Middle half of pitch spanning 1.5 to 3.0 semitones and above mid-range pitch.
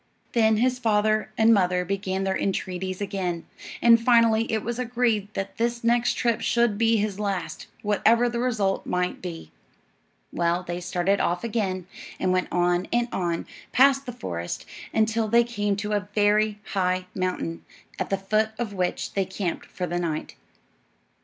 No: average, 3.9 semitones; high, 205 Hz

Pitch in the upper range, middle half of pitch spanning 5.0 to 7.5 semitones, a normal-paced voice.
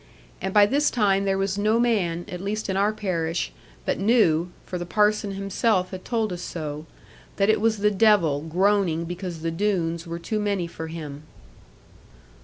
No: high, 195 Hz; average, 3.7 semitones; average, 180 wpm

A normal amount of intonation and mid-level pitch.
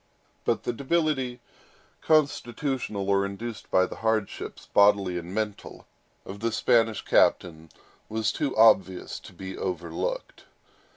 No: average, 4.0 semitones; low, 110 Hz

